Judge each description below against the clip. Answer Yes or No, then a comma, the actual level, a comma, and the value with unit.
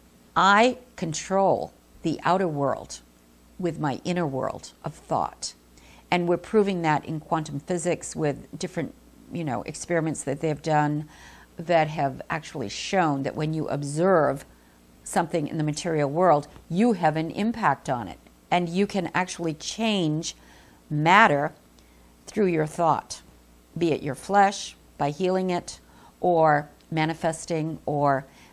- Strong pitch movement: Yes, wide, 6.6 semitones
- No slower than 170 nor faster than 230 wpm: No, slow, 135 wpm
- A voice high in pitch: No, medium, 155 Hz